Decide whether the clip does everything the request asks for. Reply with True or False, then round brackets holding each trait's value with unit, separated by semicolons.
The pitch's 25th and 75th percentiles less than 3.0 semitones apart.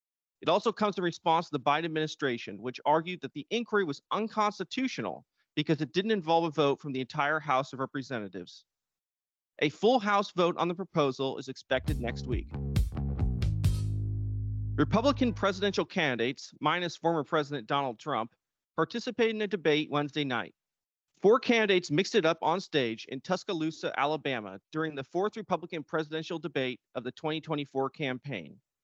False (5.6 semitones)